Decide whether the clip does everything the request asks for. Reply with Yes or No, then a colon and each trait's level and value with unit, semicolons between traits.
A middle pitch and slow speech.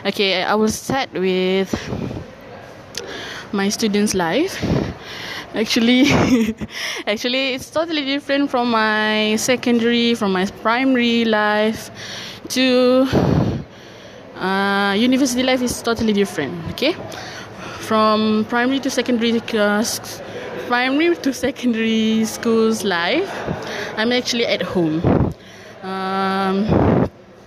No: high, 225 Hz; slow, 95 wpm